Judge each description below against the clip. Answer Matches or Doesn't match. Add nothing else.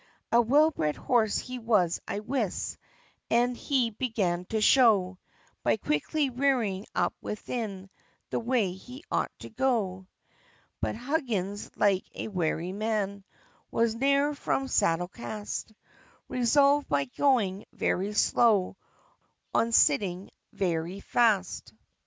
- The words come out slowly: Matches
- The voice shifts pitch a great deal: Doesn't match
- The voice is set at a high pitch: Matches